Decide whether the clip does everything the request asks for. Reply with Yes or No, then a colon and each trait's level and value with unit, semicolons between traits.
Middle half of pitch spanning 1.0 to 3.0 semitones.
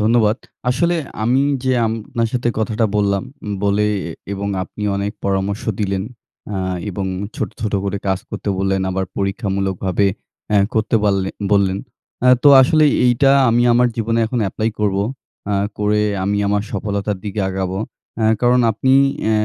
Yes: average, 2.7 semitones